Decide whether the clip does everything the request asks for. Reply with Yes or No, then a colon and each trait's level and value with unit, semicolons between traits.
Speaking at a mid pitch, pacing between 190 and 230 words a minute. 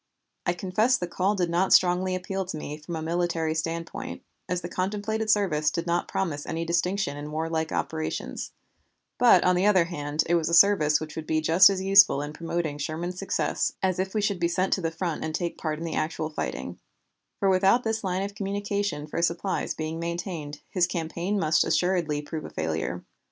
Yes: medium, 175 Hz; average, 200 wpm